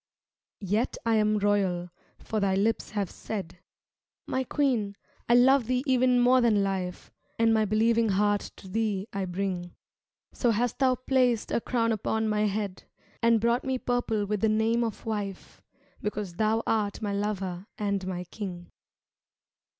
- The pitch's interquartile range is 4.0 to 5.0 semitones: No, average, 2.8 semitones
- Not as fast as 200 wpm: Yes, average, 160 wpm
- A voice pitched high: Yes, high, 215 Hz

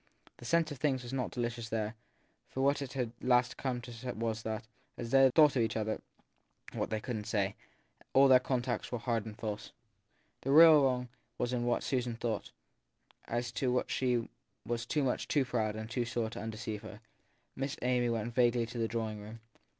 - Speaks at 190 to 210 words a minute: Yes, average, 200 wpm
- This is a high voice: No, low, 120 Hz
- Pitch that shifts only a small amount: Yes, narrow, 2.3 semitones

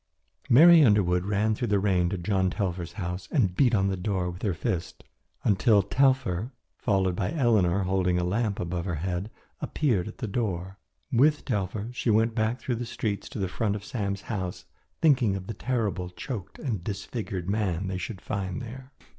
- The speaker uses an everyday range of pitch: Yes, average, 3.8 semitones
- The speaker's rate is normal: Yes, average, 185 wpm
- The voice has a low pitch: Yes, low, 100 Hz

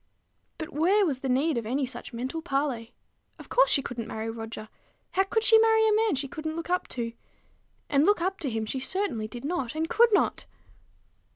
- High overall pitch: Yes, very high, 295 Hz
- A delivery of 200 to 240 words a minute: Yes, fast, 205 wpm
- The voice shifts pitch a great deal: Yes, wide, 7.9 semitones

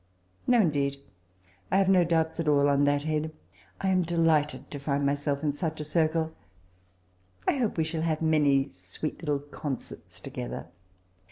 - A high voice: No, medium, 150 Hz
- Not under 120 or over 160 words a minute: No, average, 175 wpm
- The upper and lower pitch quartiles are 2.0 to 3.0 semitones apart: Yes, narrow, 2.5 semitones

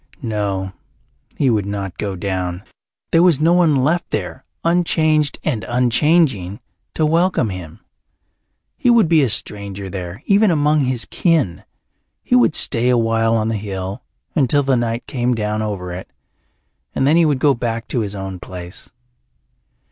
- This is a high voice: No, low, 120 Hz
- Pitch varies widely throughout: Yes, wide, 7.3 semitones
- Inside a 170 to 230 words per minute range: No, average, 155 wpm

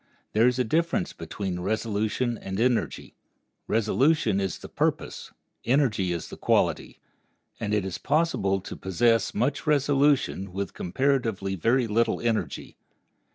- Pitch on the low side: Yes, low, 115 Hz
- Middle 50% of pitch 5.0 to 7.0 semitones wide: Yes, average, 5.3 semitones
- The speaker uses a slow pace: Yes, slow, 130 wpm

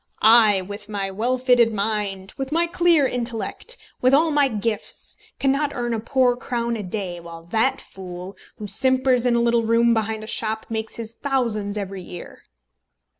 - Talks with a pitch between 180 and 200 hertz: No, high, 230 Hz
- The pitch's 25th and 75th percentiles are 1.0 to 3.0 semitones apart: No, average, 3.8 semitones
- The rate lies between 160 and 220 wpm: Yes, average, 175 wpm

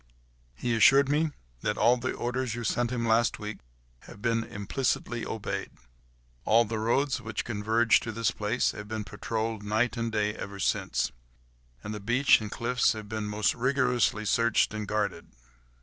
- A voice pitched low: Yes, low, 115 Hz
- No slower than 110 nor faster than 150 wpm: No, average, 165 wpm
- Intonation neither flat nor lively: No, narrow, 2.3 semitones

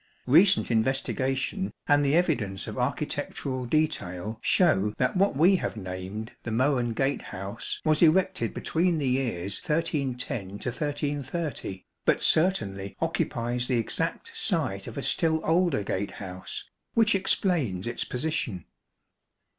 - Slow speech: Yes, slow, 120 wpm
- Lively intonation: Yes, wide, 7.0 semitones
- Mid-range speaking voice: No, low, 130 Hz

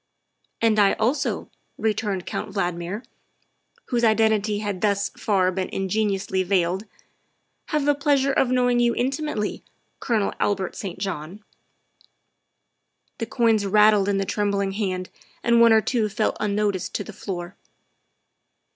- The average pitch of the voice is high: Yes, high, 210 Hz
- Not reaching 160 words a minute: Yes, average, 140 wpm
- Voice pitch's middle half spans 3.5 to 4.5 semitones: No, average, 2.9 semitones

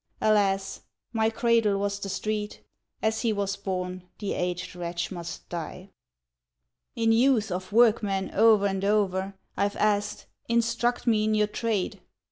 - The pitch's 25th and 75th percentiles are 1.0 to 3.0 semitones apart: Yes, narrow, 2.4 semitones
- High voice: Yes, high, 205 Hz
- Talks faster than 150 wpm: No, average, 140 wpm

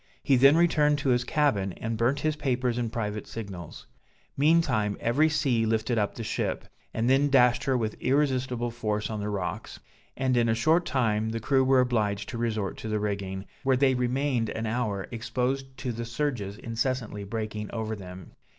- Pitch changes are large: No, average, 3.7 semitones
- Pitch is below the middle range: Yes, low, 120 Hz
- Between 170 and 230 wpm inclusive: Yes, average, 185 wpm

